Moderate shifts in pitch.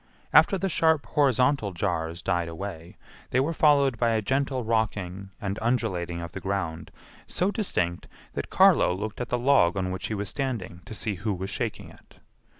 No: wide, 6.4 semitones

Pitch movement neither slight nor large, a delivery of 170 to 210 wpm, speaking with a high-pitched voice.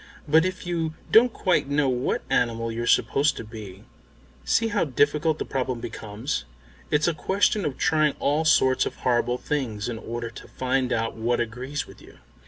No: average, 4.7 semitones; average, 180 wpm; low, 130 Hz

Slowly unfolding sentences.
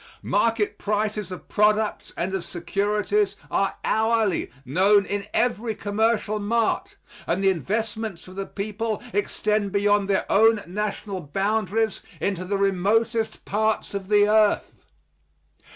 Yes: slow, 125 wpm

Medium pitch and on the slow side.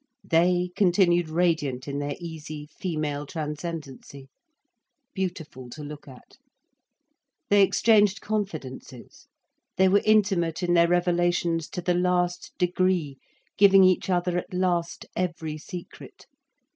Yes: medium, 175 Hz; slow, 115 wpm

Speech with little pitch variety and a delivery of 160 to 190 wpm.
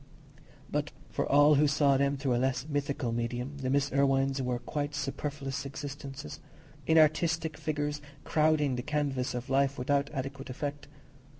No: narrow, 1.7 semitones; average, 140 wpm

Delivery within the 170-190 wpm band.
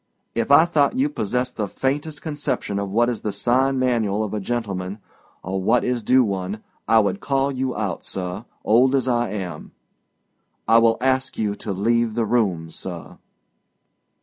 Yes: average, 175 wpm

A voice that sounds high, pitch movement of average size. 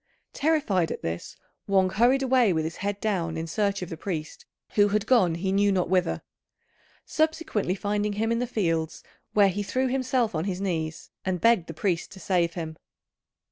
Yes: high, 195 Hz; average, 4.5 semitones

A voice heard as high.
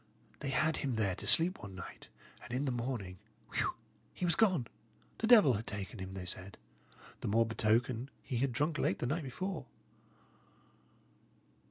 No: low, 125 Hz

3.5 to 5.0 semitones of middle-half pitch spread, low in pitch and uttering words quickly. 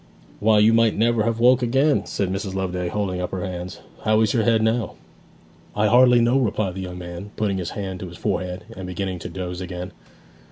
Yes: average, 3.8 semitones; low, 100 Hz; fast, 210 wpm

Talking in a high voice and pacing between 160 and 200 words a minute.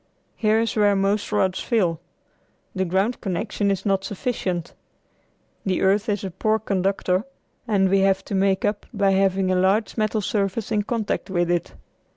Yes: high, 195 Hz; average, 170 wpm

